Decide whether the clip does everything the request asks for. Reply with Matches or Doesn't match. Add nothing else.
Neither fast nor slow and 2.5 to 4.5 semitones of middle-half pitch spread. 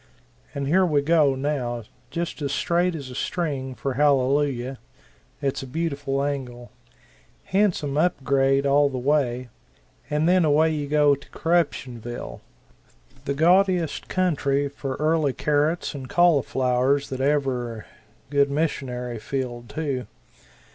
Doesn't match